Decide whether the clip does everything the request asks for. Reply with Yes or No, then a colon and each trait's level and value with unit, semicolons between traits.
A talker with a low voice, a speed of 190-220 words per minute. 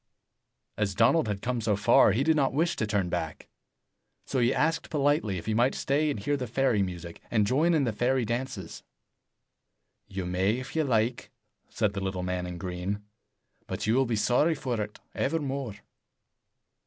No: low, 115 Hz; average, 180 wpm